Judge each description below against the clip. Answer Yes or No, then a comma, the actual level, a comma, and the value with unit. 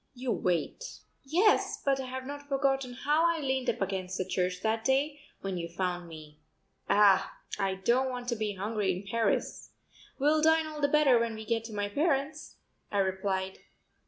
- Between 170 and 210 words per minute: Yes, average, 185 wpm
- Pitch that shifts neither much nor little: No, wide, 6.4 semitones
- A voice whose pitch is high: Yes, high, 230 Hz